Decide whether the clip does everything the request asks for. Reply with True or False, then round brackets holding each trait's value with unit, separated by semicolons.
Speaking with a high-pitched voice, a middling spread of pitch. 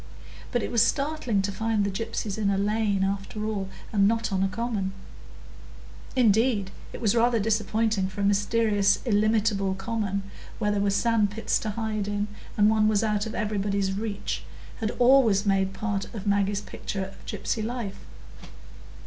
False (210 Hz; 2.0 semitones)